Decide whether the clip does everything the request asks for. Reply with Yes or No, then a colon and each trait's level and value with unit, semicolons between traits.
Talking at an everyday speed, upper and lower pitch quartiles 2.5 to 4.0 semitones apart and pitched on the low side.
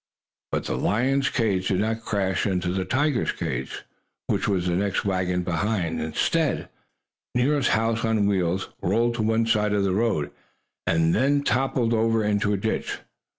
Yes: average, 155 wpm; average, 3.6 semitones; low, 105 Hz